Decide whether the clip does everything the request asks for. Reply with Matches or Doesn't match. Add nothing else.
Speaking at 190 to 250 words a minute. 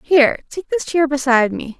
Matches